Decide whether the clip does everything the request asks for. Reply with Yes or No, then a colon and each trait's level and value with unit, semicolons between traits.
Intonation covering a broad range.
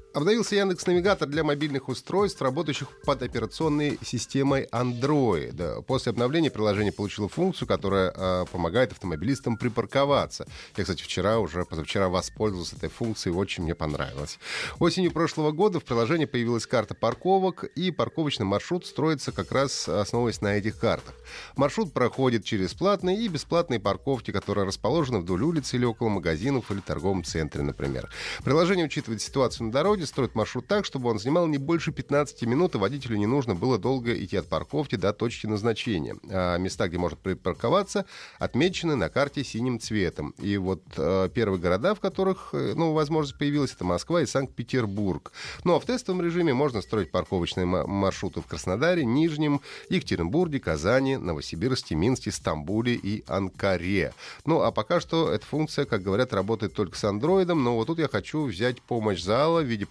Yes: wide, 7.2 semitones